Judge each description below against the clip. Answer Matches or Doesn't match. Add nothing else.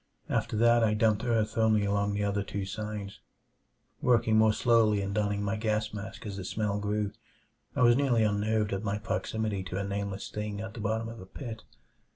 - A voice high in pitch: Doesn't match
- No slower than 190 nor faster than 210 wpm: Matches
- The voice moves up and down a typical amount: Doesn't match